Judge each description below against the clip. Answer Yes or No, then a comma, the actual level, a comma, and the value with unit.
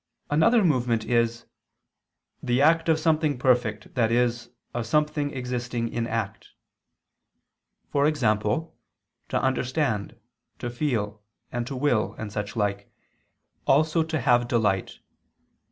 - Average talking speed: No, slow, 110 wpm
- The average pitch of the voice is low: Yes, low, 125 Hz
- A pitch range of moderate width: Yes, average, 4.6 semitones